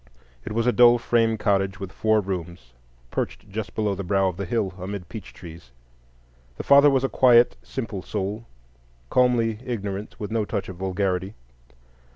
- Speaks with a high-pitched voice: No, low, 105 Hz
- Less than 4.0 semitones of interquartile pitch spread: Yes, average, 3.3 semitones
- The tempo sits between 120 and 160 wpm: No, average, 170 wpm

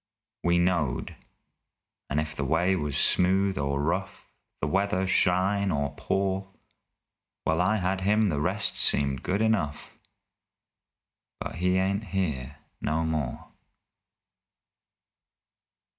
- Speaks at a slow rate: Yes, slow, 115 wpm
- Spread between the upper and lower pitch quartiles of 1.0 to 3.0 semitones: No, average, 4.2 semitones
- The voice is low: Yes, very low, 90 Hz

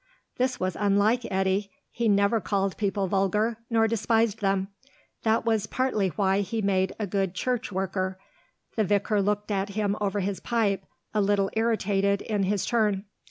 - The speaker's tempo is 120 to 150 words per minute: No, average, 160 wpm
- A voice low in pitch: No, high, 205 Hz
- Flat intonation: Yes, narrow, 2.2 semitones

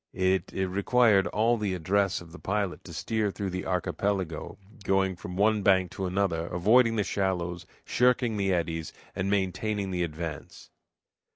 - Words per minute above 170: No, average, 155 wpm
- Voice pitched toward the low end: Yes, very low, 95 Hz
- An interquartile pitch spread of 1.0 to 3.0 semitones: Yes, narrow, 2.4 semitones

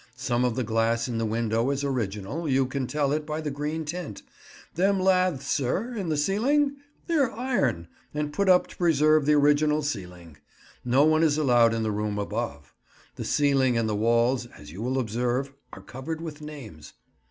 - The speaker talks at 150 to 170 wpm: No, average, 185 wpm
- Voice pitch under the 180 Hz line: Yes, low, 135 Hz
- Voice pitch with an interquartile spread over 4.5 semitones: Yes, average, 5.1 semitones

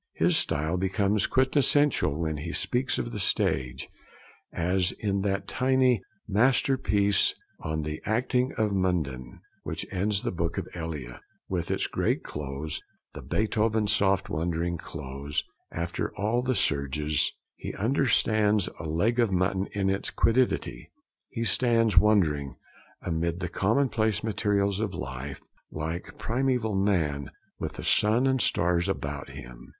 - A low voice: Yes, very low, 95 Hz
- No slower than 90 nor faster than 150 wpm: Yes, slow, 135 wpm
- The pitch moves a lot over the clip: Yes, wide, 5.8 semitones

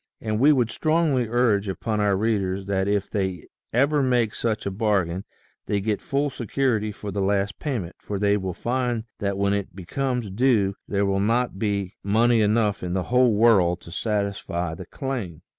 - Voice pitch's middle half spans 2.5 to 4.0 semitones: Yes, average, 3.5 semitones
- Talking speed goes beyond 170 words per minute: Yes, average, 180 wpm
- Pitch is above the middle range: No, low, 105 Hz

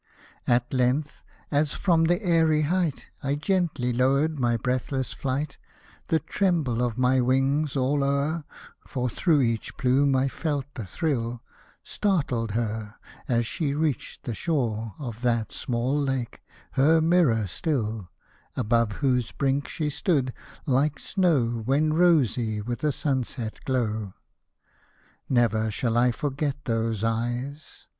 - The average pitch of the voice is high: No, low, 130 Hz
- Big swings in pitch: No, average, 4.2 semitones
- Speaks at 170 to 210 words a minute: No, slow, 135 wpm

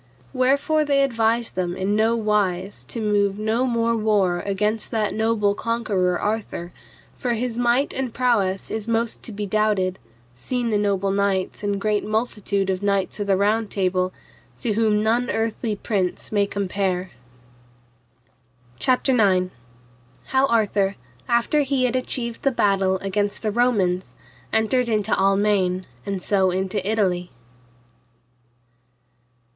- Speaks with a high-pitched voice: Yes, high, 210 Hz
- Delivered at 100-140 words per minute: Yes, slow, 135 wpm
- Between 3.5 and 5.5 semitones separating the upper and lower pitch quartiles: No, average, 3.0 semitones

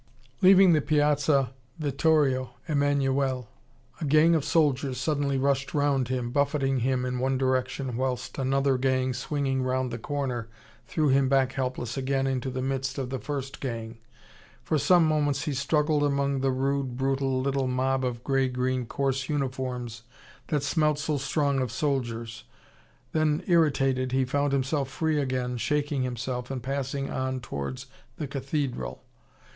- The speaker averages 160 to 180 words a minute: No, average, 150 wpm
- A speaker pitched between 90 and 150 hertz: Yes, low, 135 Hz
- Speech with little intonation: Yes, narrow, 1.9 semitones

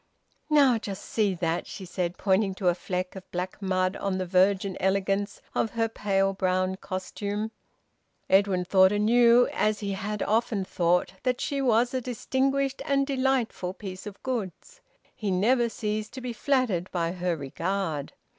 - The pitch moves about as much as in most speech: Yes, average, 3.9 semitones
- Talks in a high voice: Yes, high, 200 Hz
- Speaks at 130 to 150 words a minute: No, average, 160 wpm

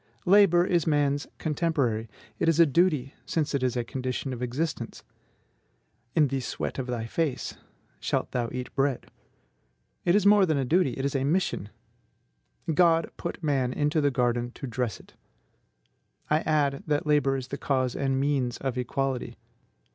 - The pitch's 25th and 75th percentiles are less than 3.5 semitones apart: No, average, 3.8 semitones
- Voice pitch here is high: No, medium, 140 Hz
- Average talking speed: Yes, average, 170 wpm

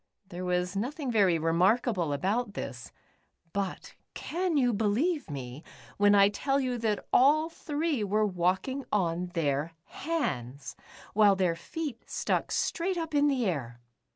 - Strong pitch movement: Yes, wide, 8.0 semitones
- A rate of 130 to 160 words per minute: Yes, average, 140 wpm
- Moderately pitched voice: No, high, 205 Hz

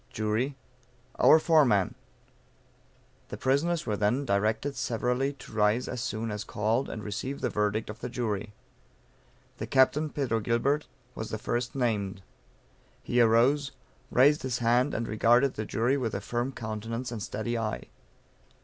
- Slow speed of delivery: No, average, 150 wpm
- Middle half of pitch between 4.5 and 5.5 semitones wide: No, average, 3.5 semitones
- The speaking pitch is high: No, low, 120 Hz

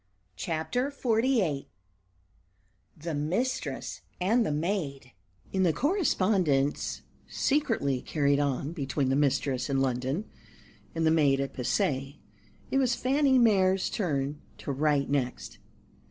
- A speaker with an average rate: No, slow, 115 wpm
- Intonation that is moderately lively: No, wide, 7.6 semitones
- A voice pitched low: No, medium, 150 Hz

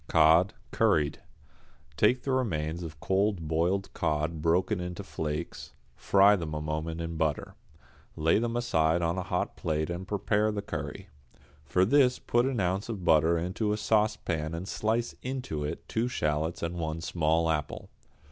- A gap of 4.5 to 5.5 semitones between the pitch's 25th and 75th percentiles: Yes, average, 4.8 semitones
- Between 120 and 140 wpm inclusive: No, average, 160 wpm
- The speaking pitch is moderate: No, very low, 85 Hz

